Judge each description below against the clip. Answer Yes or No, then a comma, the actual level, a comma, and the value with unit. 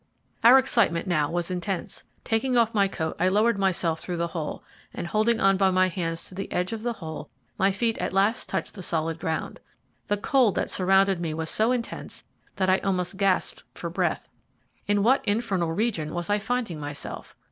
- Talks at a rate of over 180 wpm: Yes, average, 195 wpm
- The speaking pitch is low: No, high, 190 Hz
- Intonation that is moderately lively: Yes, average, 4.2 semitones